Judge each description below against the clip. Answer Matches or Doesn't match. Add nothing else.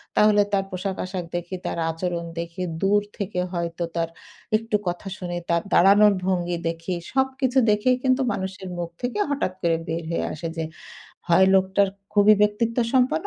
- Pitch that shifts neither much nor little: Matches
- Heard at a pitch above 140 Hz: Matches